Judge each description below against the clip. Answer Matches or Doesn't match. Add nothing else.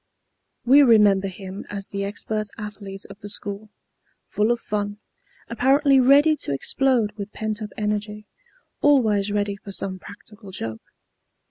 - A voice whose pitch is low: Doesn't match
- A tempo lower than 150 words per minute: Matches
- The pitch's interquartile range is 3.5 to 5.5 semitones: Doesn't match